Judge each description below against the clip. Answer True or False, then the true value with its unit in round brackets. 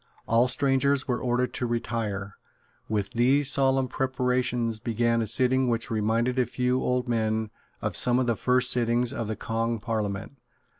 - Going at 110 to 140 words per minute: False (160 wpm)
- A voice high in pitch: False (120 Hz)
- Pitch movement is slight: True (2.0 semitones)